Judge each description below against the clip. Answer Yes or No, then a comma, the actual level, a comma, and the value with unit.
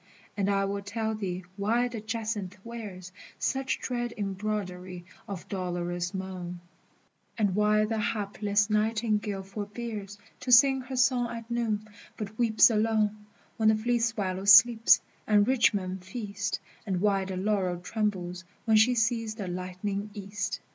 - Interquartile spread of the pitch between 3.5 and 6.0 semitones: No, average, 2.7 semitones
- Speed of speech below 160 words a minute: Yes, average, 145 wpm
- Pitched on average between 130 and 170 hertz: No, high, 210 Hz